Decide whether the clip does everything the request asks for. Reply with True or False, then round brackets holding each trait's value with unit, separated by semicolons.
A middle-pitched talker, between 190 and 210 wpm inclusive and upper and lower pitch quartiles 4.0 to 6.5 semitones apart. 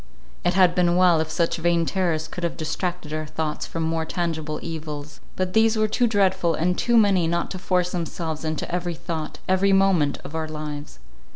False (170 Hz; 195 wpm; 2.6 semitones)